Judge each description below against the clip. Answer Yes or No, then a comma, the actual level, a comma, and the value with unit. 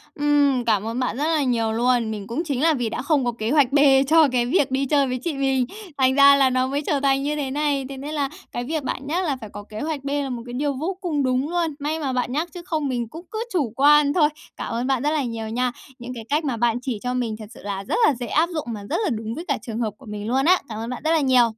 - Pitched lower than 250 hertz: No, very high, 270 Hz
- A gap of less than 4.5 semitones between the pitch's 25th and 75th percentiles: Yes, average, 3.6 semitones